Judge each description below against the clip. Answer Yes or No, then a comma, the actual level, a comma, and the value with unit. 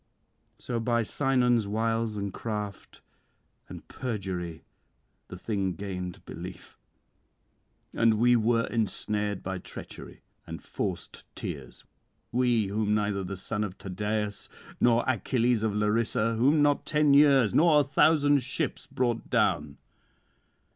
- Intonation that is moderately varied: Yes, average, 3.3 semitones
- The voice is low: Yes, low, 110 Hz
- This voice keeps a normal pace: No, slow, 120 wpm